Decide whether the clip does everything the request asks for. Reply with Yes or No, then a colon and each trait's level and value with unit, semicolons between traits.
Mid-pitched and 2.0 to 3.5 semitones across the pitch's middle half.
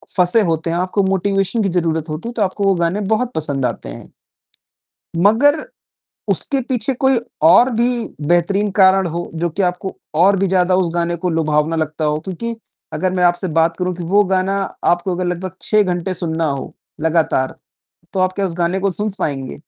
Yes: medium, 180 Hz; average, 2.9 semitones